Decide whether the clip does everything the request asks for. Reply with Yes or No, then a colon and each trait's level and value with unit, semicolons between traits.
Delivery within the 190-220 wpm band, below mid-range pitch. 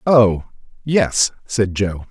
No: slow, 115 wpm; low, 110 Hz